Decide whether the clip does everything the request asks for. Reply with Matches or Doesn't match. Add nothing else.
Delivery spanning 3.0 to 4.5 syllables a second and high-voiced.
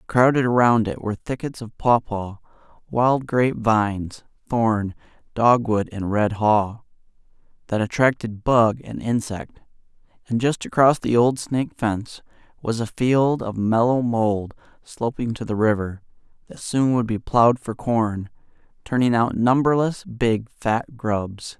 Doesn't match